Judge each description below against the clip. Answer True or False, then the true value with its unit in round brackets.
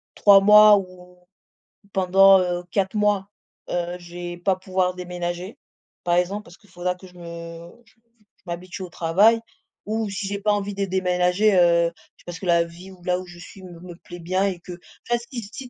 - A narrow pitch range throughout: True (2.2 semitones)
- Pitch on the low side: False (180 Hz)